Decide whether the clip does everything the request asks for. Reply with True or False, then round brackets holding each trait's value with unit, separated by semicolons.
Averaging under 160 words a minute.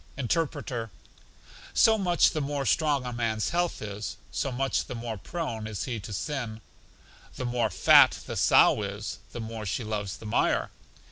False (165 wpm)